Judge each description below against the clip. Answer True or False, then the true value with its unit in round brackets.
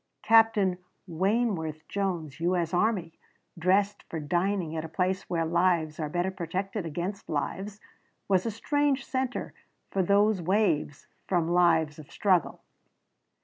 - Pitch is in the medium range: True (180 Hz)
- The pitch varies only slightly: False (3.6 semitones)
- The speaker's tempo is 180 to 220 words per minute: False (135 wpm)